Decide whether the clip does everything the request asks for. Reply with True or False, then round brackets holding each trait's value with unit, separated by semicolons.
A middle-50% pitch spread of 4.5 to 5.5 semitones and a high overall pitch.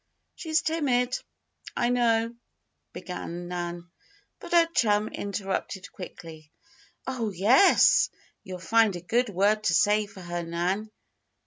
True (5.2 semitones; 205 Hz)